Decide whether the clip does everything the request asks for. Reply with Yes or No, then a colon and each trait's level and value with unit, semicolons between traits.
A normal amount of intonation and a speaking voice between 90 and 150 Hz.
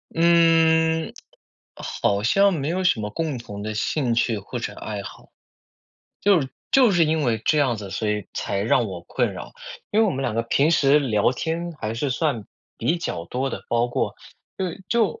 No: wide, 7.1 semitones; low, 135 Hz